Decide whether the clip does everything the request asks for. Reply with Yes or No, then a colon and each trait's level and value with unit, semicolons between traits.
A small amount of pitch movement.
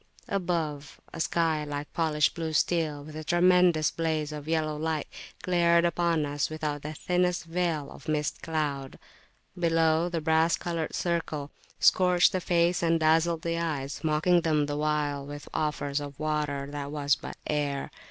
Yes: narrow, 2.2 semitones